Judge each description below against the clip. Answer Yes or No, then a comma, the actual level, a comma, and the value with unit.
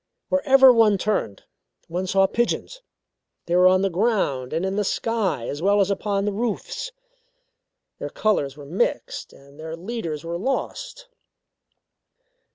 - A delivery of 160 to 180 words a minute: No, average, 145 wpm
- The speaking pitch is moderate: No, high, 195 Hz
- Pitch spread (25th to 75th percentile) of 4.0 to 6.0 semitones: Yes, wide, 5.5 semitones